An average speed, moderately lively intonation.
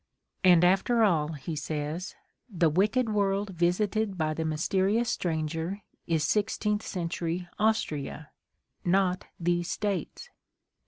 No: slow, 125 wpm; average, 4.2 semitones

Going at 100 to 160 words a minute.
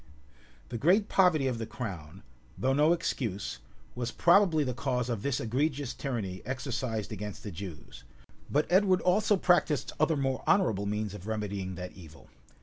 Yes: average, 155 wpm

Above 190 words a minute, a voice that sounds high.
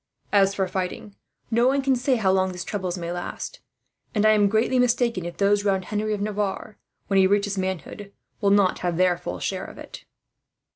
Yes: average, 200 wpm; high, 200 Hz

